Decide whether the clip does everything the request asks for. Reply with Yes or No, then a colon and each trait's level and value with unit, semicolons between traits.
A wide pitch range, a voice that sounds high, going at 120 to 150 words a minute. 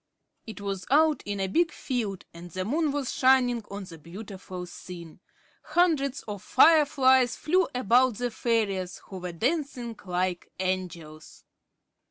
Yes: wide, 6.2 semitones; high, 220 Hz; average, 140 wpm